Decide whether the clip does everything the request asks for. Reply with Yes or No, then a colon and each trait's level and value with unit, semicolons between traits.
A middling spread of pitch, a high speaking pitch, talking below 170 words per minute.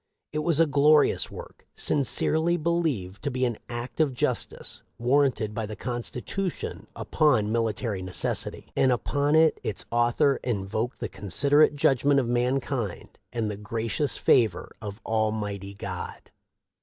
No: average, 5.0 semitones; low, 120 Hz; average, 145 wpm